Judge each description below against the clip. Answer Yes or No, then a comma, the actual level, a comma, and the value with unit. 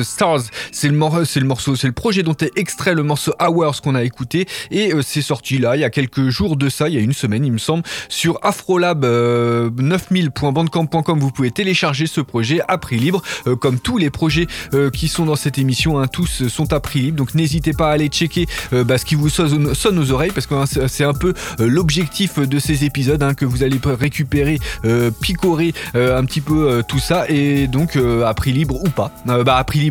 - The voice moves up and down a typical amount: Yes, average, 3.5 semitones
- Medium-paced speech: No, fast, 240 wpm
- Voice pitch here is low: No, medium, 145 Hz